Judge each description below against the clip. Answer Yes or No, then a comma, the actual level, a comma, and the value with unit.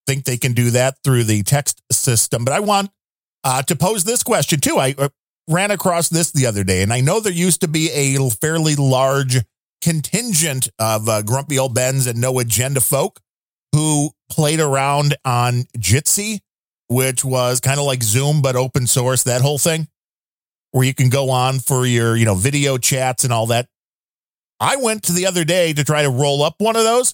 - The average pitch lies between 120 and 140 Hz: Yes, low, 135 Hz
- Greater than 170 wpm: Yes, average, 200 wpm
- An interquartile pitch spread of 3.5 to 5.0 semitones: Yes, average, 3.9 semitones